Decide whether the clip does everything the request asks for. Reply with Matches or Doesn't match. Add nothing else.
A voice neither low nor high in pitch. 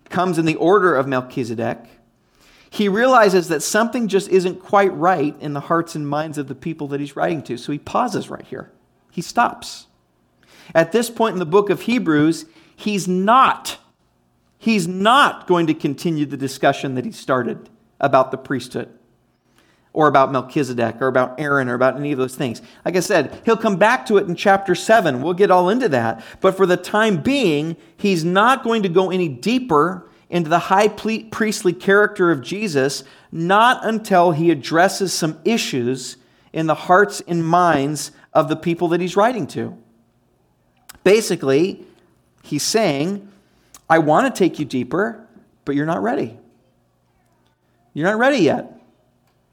Matches